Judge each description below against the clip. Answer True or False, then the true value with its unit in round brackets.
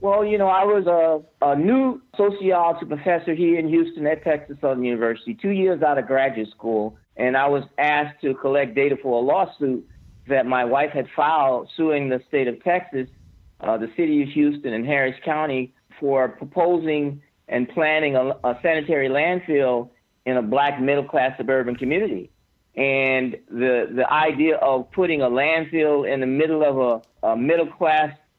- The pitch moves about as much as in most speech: True (3.9 semitones)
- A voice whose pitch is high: False (140 Hz)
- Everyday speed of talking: True (175 wpm)